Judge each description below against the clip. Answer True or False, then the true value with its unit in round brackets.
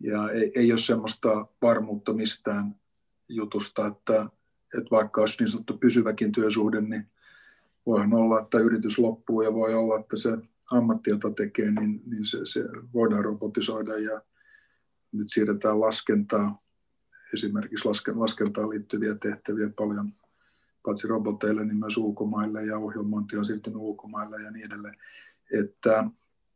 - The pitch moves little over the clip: True (1.2 semitones)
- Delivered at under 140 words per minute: True (130 wpm)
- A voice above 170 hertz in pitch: False (110 Hz)